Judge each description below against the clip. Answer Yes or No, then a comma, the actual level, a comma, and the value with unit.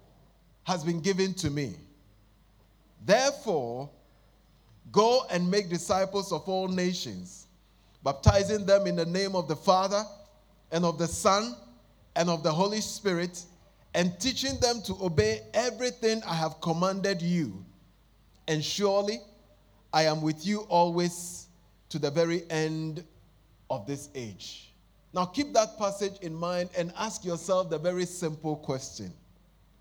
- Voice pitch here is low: No, medium, 175 Hz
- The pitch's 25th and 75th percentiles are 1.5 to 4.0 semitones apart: No, average, 5.0 semitones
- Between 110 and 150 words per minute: Yes, slow, 135 wpm